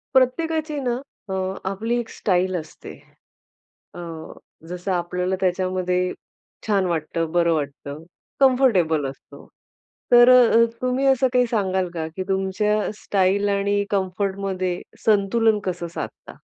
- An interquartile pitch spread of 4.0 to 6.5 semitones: Yes, average, 4.3 semitones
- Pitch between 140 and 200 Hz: Yes, high, 190 Hz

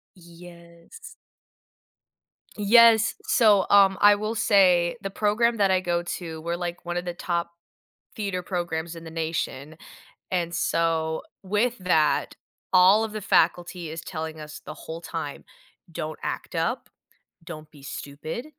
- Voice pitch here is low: No, medium, 175 Hz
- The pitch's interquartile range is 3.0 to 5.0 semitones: Yes, average, 3.6 semitones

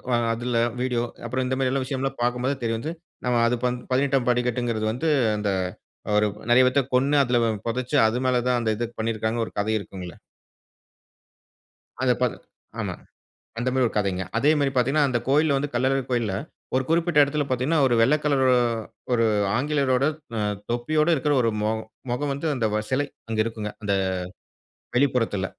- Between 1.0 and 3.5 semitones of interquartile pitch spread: Yes, average, 2.8 semitones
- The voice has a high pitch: No, low, 125 Hz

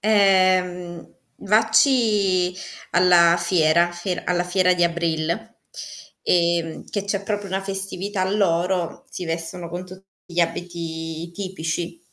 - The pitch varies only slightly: Yes, narrow, 2.2 semitones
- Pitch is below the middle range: No, medium, 180 Hz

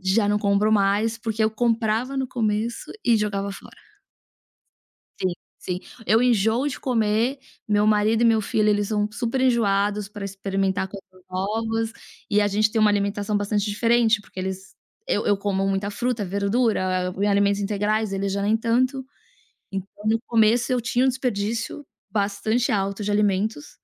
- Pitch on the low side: No, high, 210 Hz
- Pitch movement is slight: Yes, narrow, 2.2 semitones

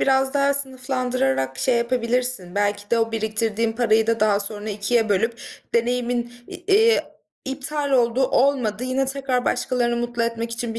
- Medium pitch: No, high, 235 Hz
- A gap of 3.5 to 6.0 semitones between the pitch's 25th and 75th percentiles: No, narrow, 2.6 semitones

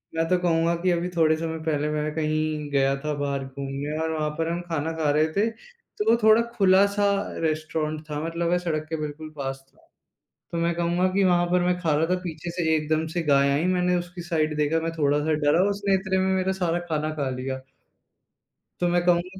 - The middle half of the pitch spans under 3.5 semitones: Yes, average, 2.8 semitones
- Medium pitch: Yes, medium, 165 Hz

